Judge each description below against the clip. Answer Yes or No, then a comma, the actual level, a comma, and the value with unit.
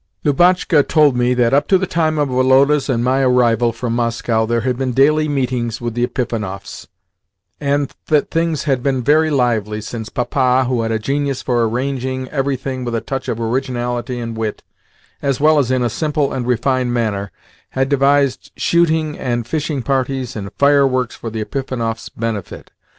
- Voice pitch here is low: Yes, low, 130 Hz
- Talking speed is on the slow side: No, average, 175 wpm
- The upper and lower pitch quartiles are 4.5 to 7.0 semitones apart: No, average, 3.0 semitones